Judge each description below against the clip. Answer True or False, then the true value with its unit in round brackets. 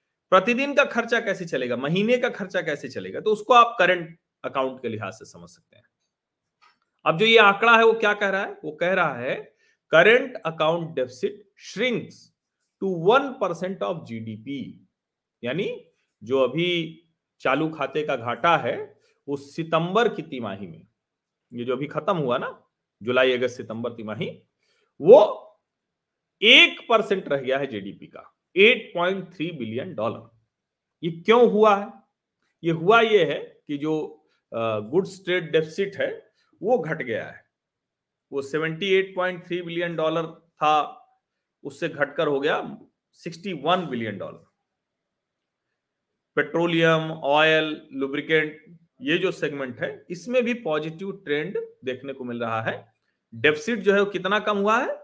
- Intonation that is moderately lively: False (6.2 semitones)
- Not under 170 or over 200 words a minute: False (130 wpm)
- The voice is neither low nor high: True (170 Hz)